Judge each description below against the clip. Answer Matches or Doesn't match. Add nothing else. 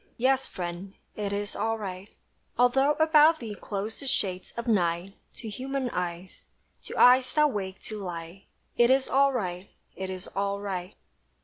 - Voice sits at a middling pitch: Doesn't match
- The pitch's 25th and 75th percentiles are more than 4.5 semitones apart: Matches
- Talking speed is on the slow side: Doesn't match